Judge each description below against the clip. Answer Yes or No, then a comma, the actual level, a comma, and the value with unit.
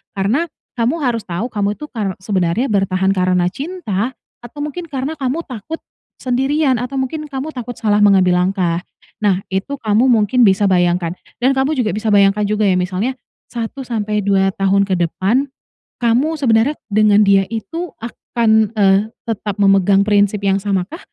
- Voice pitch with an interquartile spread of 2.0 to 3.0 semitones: No, average, 4.8 semitones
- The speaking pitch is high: Yes, high, 215 Hz